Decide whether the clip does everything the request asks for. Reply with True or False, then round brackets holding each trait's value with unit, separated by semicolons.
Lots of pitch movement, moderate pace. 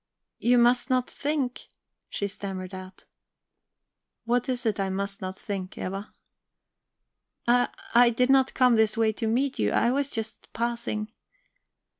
False (3.8 semitones; 145 wpm)